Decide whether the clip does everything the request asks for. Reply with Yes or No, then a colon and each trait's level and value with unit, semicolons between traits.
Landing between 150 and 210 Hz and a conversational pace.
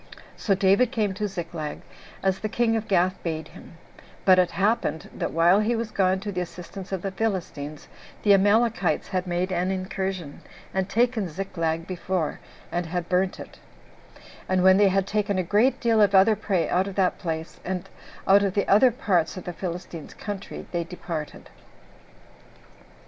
Yes: high, 190 Hz; average, 175 wpm